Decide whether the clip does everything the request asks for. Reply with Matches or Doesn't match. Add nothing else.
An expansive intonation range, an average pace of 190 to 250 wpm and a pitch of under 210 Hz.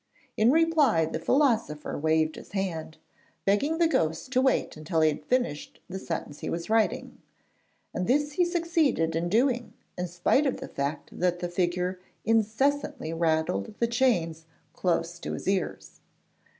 Doesn't match